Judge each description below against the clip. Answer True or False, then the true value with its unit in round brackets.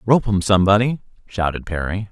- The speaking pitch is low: True (100 Hz)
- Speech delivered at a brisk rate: False (140 wpm)